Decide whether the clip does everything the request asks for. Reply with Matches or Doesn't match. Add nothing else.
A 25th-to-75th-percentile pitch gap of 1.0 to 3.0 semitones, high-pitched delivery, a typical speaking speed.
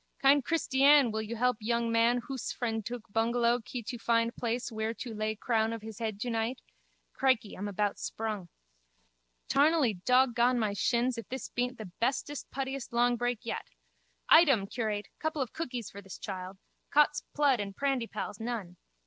Matches